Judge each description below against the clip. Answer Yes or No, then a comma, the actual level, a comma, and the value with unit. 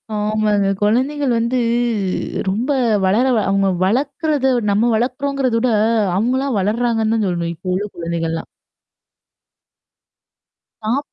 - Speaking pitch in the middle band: No, high, 225 Hz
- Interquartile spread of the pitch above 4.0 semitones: Yes, average, 4.6 semitones